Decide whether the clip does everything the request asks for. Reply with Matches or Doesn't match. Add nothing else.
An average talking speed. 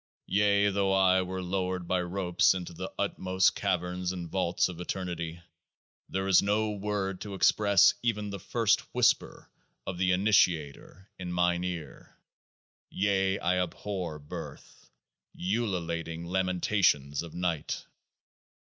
Doesn't match